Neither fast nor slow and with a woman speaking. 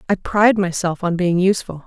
Yes: average, 195 wpm; female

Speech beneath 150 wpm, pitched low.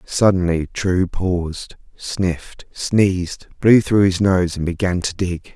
Yes: average, 140 wpm; very low, 90 Hz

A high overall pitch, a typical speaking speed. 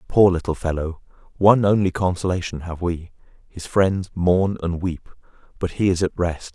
No: very low, 90 Hz; average, 165 wpm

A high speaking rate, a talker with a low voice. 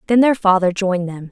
No: fast, 230 wpm; high, 195 Hz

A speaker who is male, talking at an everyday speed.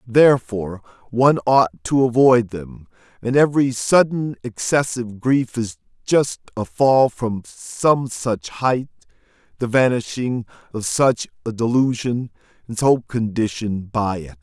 No: male; slow, 125 wpm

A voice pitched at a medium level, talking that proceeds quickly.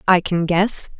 No: medium, 180 Hz; average, 180 wpm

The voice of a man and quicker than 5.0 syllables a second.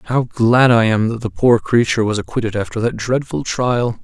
Yes: male; 5.2 syllables/s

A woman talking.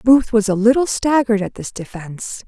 Yes: female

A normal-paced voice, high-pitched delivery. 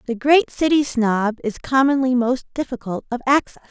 Yes: average, 160 wpm; very high, 255 Hz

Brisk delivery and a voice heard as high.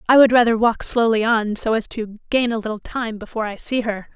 Yes: fast, 245 wpm; high, 225 Hz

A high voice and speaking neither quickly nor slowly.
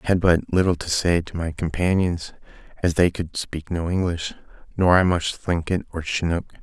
No: very low, 85 Hz; average, 190 wpm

